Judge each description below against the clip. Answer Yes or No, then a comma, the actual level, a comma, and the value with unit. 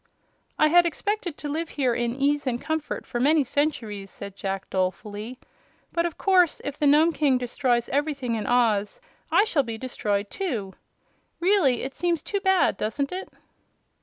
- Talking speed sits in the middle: Yes, average, 165 wpm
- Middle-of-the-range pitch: No, very high, 275 Hz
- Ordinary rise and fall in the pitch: No, wide, 5.7 semitones